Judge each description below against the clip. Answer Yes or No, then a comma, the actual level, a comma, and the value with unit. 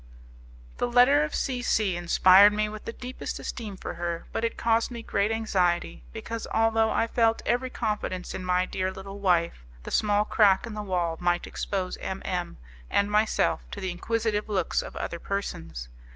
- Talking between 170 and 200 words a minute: Yes, average, 180 wpm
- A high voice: Yes, high, 205 Hz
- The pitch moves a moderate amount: Yes, average, 3.7 semitones